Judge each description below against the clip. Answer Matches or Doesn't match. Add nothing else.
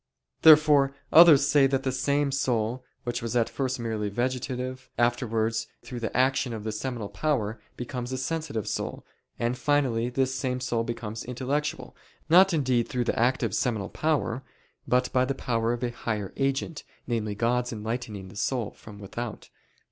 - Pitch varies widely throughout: Doesn't match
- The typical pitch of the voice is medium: Doesn't match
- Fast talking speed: Doesn't match